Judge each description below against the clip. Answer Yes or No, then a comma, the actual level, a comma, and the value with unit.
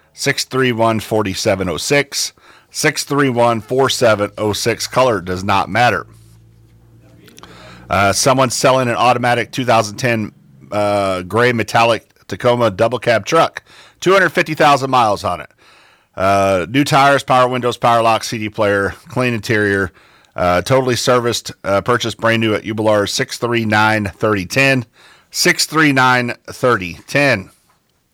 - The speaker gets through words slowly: Yes, slow, 95 wpm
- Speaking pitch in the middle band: No, low, 115 Hz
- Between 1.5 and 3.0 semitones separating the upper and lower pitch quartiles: No, average, 3.5 semitones